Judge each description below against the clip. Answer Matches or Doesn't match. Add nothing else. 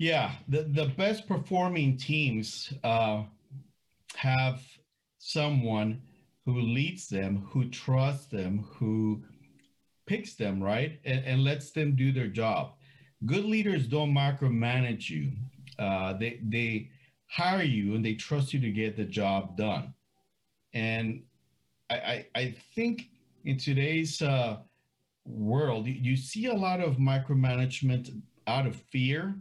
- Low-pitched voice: Matches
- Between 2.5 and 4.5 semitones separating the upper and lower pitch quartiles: Doesn't match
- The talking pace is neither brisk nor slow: Doesn't match